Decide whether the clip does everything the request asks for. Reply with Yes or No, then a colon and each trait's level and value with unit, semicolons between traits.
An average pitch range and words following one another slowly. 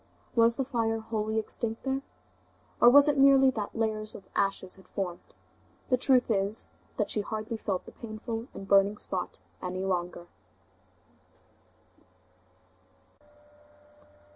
Yes: average, 3.4 semitones; slow, 125 wpm